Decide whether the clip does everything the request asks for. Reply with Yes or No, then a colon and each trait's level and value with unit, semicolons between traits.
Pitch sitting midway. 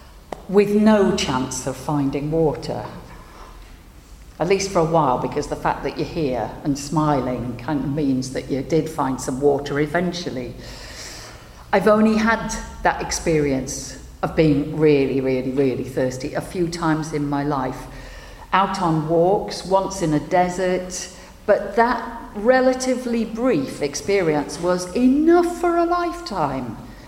Yes: medium, 155 Hz